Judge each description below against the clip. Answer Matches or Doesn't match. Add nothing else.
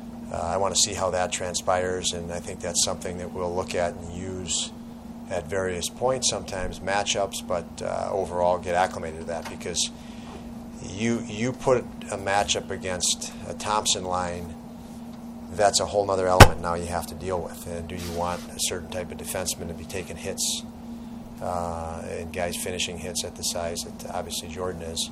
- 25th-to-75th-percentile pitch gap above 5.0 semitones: Matches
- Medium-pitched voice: Doesn't match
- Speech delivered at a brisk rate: Doesn't match